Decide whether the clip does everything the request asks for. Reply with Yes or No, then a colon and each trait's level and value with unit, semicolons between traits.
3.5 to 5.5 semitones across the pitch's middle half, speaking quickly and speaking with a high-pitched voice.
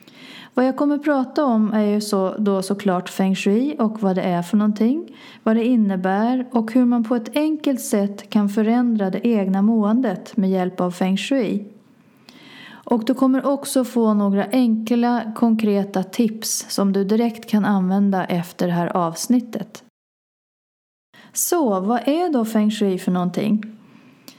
No: average, 3.9 semitones; average, 160 wpm; high, 220 Hz